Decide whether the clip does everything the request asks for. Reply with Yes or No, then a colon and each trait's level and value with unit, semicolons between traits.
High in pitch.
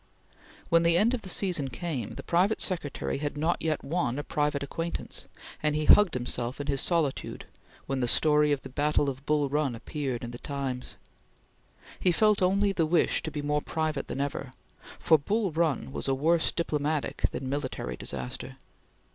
No: medium, 150 Hz